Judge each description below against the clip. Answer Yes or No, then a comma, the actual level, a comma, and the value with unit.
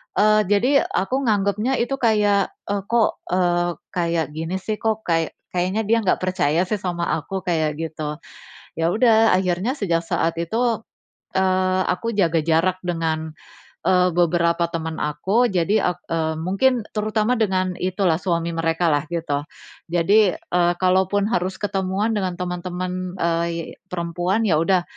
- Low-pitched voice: No, medium, 180 Hz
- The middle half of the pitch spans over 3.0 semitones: Yes, average, 3.4 semitones